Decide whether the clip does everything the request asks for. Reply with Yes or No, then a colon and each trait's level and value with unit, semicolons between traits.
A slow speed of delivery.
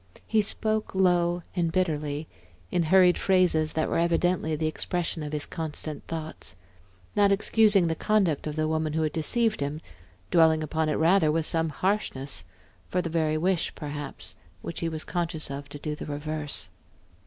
No: average, 170 wpm